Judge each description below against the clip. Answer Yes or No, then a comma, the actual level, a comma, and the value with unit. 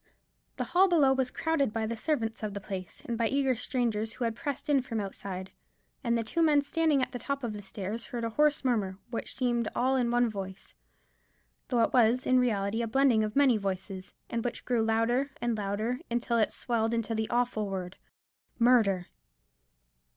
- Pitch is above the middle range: Yes, high, 235 Hz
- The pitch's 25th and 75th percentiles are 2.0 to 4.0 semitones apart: Yes, average, 3.1 semitones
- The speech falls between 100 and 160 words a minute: No, average, 195 wpm